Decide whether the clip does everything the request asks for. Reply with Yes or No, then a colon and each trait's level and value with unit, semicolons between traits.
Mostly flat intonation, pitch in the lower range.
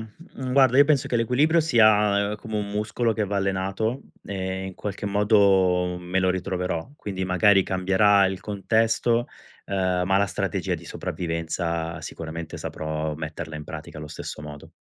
No: average, 3.3 semitones; very low, 95 Hz